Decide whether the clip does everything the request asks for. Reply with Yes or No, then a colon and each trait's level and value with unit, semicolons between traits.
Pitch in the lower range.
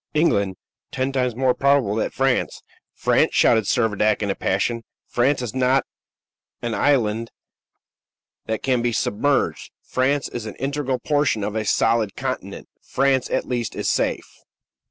Yes: low, 125 Hz